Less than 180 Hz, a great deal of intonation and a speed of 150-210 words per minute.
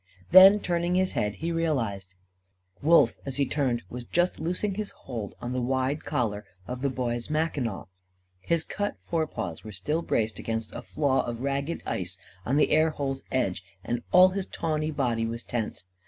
Yes: low, 135 Hz; wide, 5.8 semitones; average, 175 wpm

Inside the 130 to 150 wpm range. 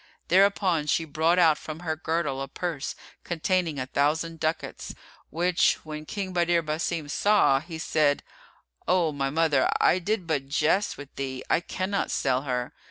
No: average, 160 wpm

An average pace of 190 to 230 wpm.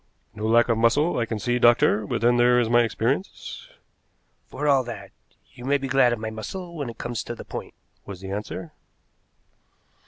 Yes: average, 195 wpm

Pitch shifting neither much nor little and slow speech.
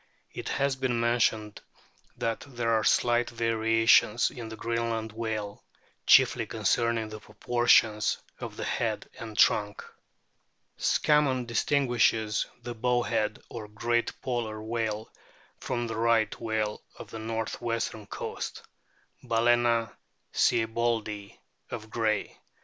No: narrow, 1.5 semitones; slow, 125 wpm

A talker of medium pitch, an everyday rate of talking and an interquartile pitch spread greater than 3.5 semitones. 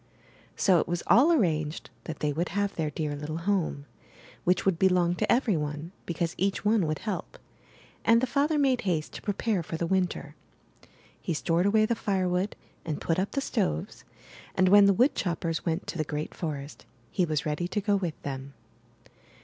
Yes: medium, 175 Hz; average, 190 wpm; average, 4.5 semitones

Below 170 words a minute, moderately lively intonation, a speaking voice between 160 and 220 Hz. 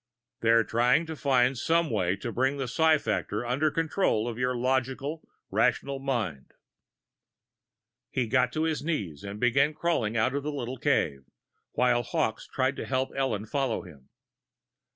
No: average, 160 wpm; average, 3.7 semitones; low, 130 Hz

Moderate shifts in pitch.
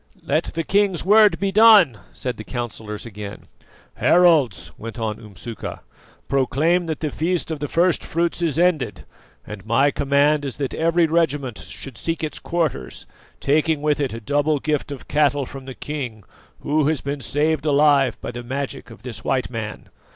Yes: average, 4.6 semitones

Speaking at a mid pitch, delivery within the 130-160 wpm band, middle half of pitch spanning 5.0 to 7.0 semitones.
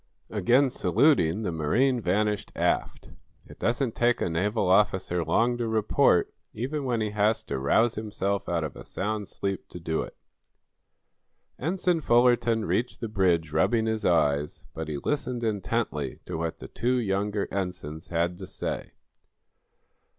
No: low, 105 Hz; average, 150 wpm; wide, 5.4 semitones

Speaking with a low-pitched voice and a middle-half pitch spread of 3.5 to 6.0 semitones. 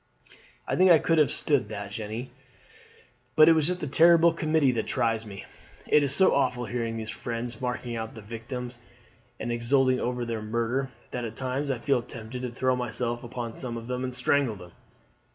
No: low, 125 Hz; average, 2.9 semitones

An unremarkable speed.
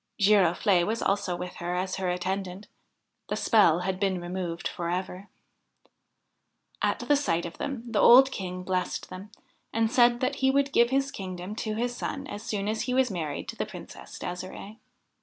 Yes: average, 175 wpm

